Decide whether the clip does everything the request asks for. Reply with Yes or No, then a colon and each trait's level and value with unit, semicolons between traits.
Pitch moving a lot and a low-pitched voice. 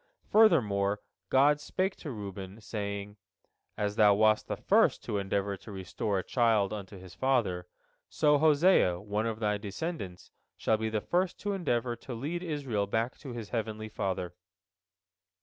No: average, 5.0 semitones; low, 110 Hz